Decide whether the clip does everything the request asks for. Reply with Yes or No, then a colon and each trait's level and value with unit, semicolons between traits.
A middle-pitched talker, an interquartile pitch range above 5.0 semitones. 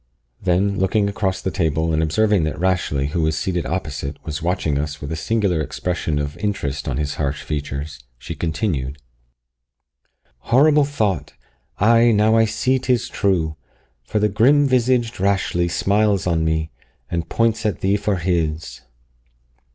No: very low, 90 Hz; wide, 5.5 semitones